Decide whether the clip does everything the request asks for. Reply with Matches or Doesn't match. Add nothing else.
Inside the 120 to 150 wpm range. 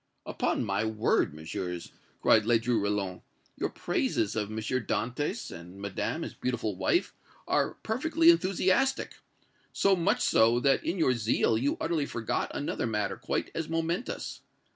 Matches